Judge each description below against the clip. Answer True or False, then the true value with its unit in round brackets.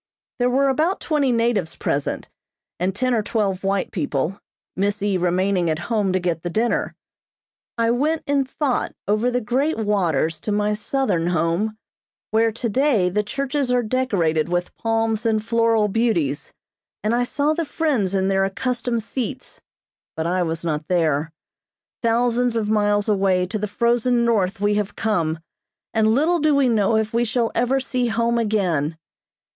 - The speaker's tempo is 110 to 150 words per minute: False (165 wpm)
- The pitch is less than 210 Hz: False (215 Hz)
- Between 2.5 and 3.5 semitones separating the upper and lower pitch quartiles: False (4.7 semitones)